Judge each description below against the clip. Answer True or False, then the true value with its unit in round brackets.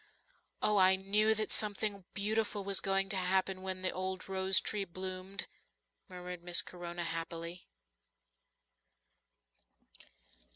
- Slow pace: True (115 wpm)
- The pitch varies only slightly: True (1.6 semitones)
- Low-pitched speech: False (190 Hz)